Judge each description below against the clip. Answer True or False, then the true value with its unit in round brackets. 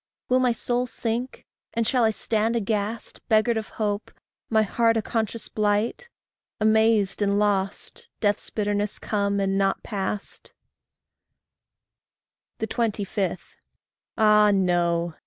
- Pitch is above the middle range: True (215 Hz)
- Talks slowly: True (115 wpm)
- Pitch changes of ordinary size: False (2.1 semitones)